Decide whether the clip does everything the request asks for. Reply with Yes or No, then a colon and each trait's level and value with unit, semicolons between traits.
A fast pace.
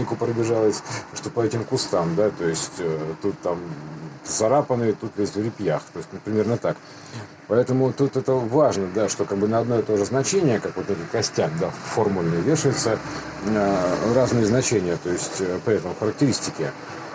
Yes: fast, 180 wpm